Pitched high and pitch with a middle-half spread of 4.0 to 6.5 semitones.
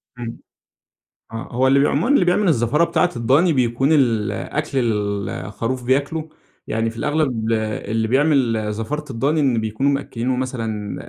No: low, 125 Hz; average, 4.3 semitones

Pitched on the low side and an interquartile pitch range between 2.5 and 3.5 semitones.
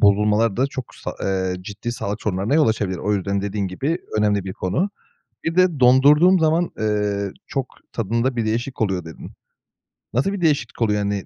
No: low, 110 Hz; average, 5.1 semitones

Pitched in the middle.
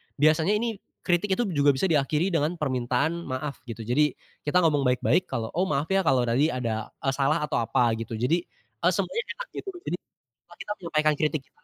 Yes: medium, 150 Hz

